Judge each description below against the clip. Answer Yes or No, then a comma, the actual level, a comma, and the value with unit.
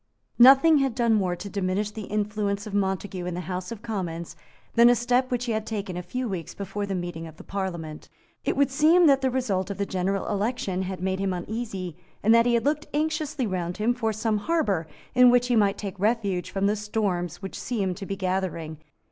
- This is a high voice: Yes, high, 205 Hz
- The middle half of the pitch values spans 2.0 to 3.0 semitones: No, average, 4.3 semitones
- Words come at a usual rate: No, fast, 220 wpm